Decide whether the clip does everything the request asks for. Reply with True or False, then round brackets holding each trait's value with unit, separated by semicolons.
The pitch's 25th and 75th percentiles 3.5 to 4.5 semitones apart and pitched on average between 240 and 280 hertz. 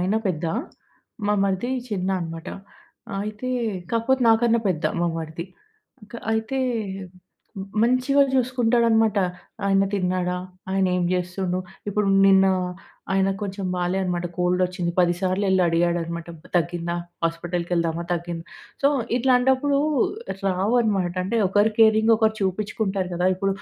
False (3.9 semitones; 190 Hz)